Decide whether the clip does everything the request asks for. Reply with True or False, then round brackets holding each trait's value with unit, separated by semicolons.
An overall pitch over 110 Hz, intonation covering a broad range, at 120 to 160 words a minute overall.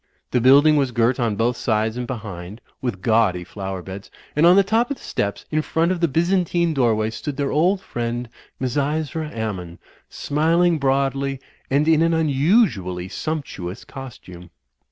False (135 Hz; 6.4 semitones; 170 wpm)